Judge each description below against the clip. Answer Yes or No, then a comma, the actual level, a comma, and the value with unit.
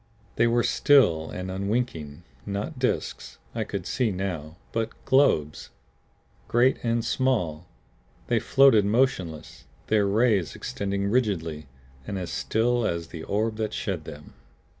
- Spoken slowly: Yes, slow, 130 wpm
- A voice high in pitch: No, low, 100 Hz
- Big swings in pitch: Yes, wide, 6.0 semitones